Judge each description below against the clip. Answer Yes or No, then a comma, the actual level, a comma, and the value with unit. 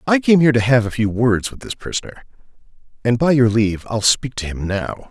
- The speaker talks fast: Yes, fast, 235 wpm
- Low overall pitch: Yes, low, 120 Hz